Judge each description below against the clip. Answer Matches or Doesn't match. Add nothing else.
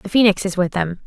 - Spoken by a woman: Matches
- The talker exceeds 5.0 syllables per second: Matches